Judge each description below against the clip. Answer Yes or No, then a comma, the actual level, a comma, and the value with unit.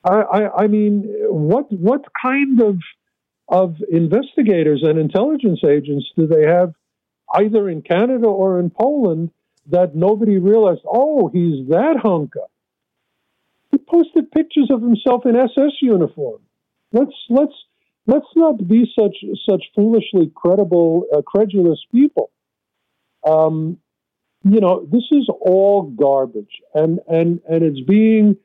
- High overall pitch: Yes, high, 205 Hz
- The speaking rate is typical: No, slow, 125 wpm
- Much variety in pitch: Yes, wide, 6.6 semitones